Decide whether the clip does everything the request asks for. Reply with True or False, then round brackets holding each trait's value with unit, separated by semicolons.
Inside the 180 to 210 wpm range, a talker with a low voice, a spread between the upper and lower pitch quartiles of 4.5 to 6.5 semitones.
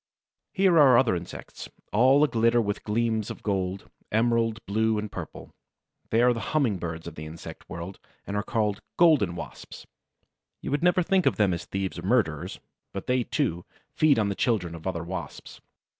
True (185 wpm; 110 Hz; 5.0 semitones)